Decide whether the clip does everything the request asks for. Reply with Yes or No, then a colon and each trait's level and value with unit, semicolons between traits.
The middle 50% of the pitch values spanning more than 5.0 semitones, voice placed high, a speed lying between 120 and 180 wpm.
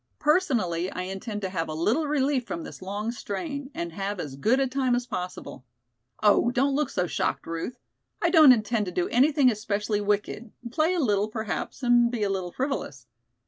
No: wide, 5.6 semitones; high, 220 Hz; average, 190 wpm